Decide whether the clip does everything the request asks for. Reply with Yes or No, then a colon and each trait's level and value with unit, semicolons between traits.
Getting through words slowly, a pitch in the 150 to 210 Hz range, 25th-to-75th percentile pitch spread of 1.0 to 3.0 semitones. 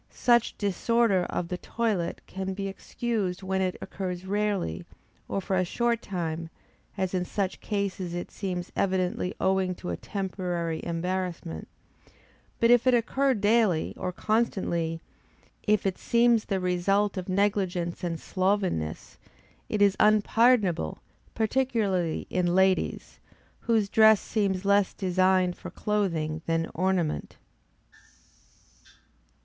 Yes: slow, 120 wpm; high, 190 Hz; average, 2.7 semitones